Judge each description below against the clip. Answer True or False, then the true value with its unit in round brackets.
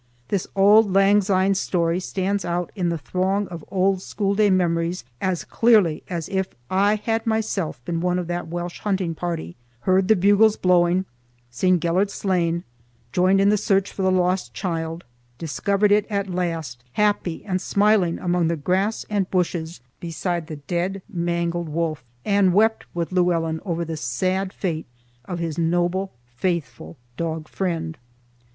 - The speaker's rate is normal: True (155 wpm)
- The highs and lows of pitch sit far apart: False (2.7 semitones)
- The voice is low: False (180 Hz)